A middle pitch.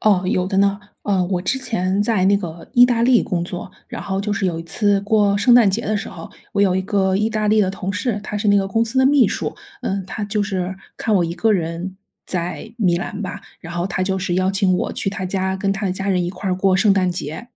No: high, 195 Hz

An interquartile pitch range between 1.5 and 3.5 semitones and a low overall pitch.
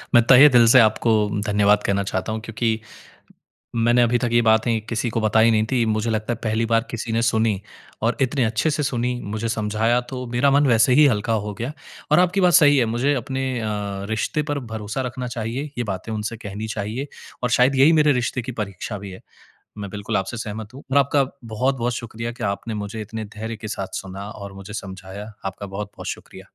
Yes: average, 2.9 semitones; low, 115 Hz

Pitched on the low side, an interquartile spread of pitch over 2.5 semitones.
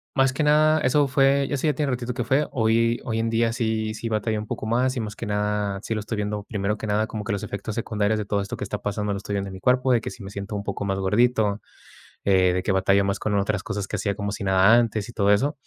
Yes: low, 105 Hz; average, 2.9 semitones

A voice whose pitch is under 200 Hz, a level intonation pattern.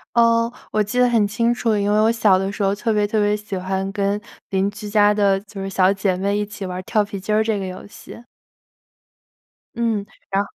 No: high, 205 Hz; narrow, 1.8 semitones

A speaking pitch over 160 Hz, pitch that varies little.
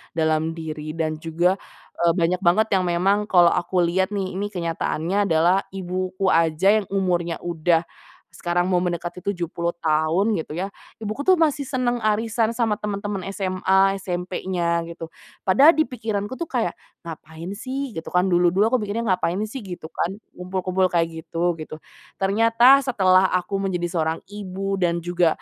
No: medium, 185 Hz; average, 3.2 semitones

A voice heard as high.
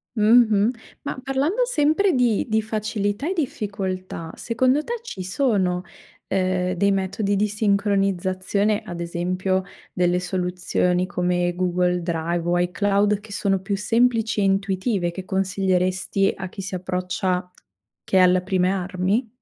Yes: high, 195 Hz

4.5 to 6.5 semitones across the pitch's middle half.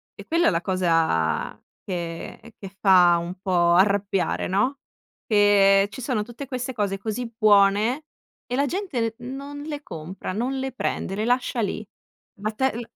Yes: average, 5.0 semitones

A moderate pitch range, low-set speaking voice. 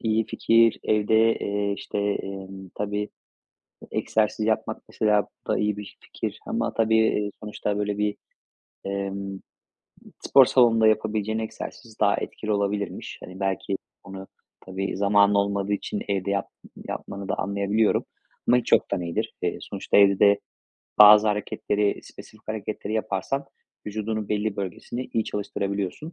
No: narrow, 1.6 semitones; low, 105 Hz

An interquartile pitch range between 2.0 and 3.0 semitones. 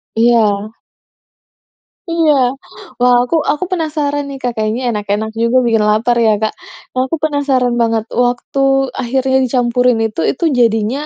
No: average, 3.7 semitones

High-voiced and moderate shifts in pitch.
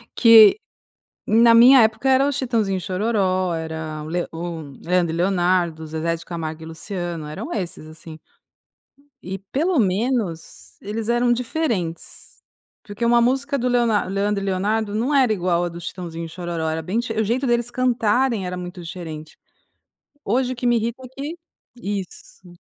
No: high, 200 Hz; wide, 5.8 semitones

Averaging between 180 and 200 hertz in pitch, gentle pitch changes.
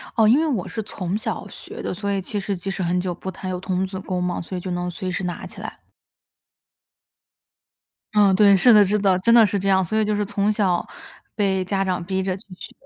Yes: high, 190 Hz; narrow, 2.2 semitones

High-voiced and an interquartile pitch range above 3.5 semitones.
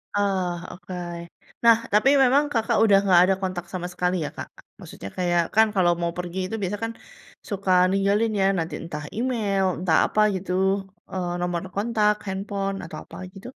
No: high, 195 Hz; average, 2.8 semitones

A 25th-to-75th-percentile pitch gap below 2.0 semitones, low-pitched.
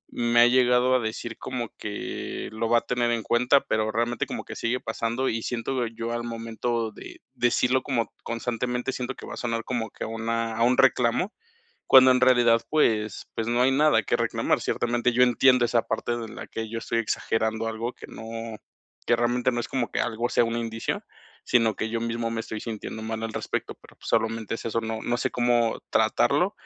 Yes: narrow, 1.4 semitones; low, 115 Hz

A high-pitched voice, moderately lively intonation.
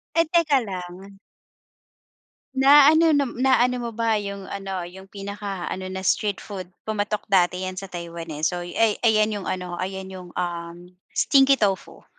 Yes: high, 195 Hz; average, 3.8 semitones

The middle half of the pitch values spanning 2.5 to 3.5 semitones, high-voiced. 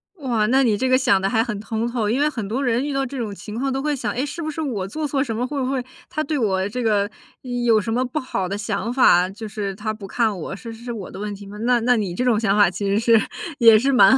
No: average, 3.9 semitones; high, 230 Hz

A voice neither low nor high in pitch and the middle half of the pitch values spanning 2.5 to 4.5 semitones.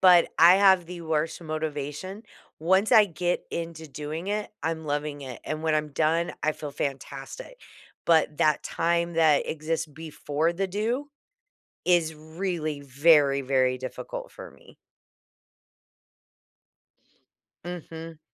Yes: medium, 160 Hz; average, 2.8 semitones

